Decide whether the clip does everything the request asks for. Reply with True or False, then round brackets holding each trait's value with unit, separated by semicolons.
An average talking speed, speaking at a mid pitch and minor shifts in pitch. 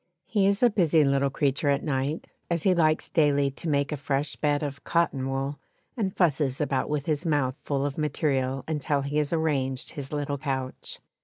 True (190 wpm; 145 Hz; 2.3 semitones)